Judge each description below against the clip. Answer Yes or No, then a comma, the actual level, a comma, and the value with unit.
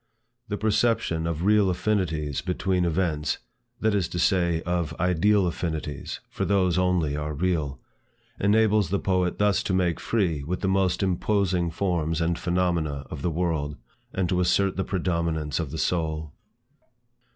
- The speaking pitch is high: No, very low, 90 Hz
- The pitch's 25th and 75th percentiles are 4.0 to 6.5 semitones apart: No, average, 3.0 semitones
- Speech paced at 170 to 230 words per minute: No, average, 150 wpm